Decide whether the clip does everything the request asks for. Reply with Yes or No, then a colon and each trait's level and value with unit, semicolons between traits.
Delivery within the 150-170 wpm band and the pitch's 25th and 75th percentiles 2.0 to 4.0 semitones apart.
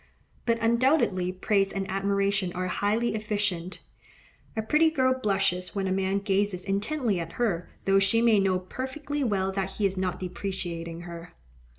Yes: average, 160 wpm; average, 3.1 semitones